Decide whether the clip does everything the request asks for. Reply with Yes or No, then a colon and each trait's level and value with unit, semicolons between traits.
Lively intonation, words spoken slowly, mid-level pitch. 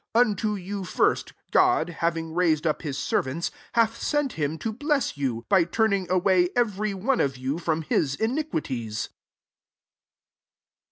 No: wide, 6.2 semitones; average, 155 wpm; medium, 180 Hz